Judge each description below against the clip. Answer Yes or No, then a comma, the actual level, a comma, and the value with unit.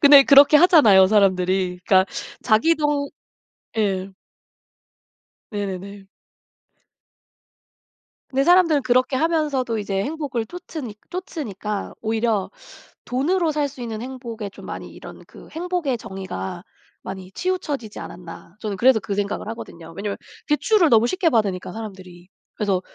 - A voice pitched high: Yes, high, 225 Hz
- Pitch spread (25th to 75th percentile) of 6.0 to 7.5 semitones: Yes, wide, 7.0 semitones